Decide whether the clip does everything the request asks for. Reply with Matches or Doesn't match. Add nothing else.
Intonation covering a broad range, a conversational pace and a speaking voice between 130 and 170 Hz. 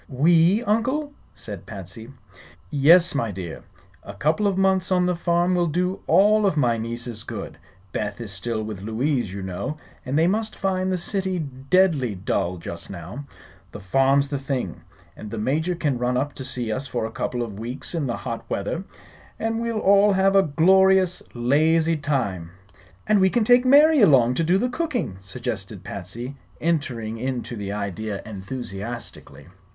Matches